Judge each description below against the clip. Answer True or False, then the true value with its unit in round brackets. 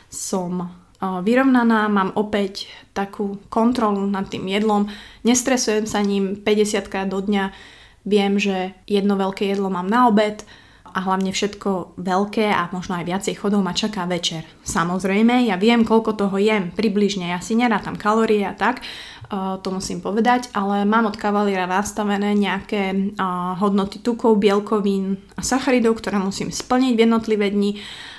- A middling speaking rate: True (145 wpm)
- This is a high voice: True (205 Hz)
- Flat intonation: True (2.2 semitones)